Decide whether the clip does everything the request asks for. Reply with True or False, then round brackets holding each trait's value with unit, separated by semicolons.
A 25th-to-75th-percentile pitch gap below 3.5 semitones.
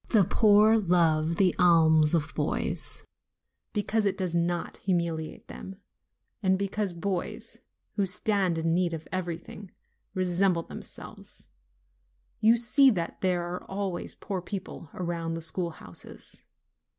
True (2.9 semitones)